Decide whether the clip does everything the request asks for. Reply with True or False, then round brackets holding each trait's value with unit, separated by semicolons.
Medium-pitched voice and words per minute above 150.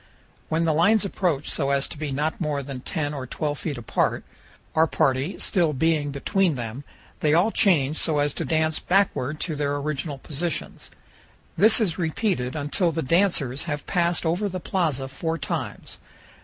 True (155 Hz; 170 wpm)